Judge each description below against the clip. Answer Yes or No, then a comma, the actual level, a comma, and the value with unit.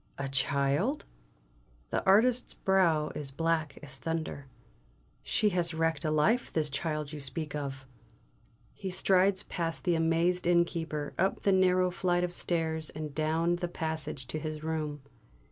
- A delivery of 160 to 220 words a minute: No, average, 145 wpm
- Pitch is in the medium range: Yes, medium, 160 Hz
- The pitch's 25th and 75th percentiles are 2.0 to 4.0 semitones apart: Yes, average, 2.8 semitones